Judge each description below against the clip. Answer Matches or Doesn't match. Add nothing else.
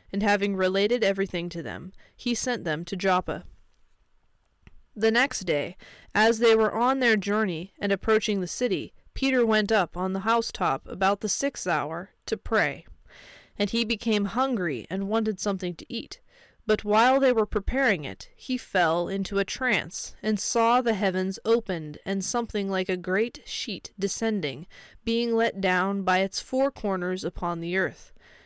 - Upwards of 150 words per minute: Matches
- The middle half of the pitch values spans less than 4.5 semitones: Matches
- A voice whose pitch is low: Doesn't match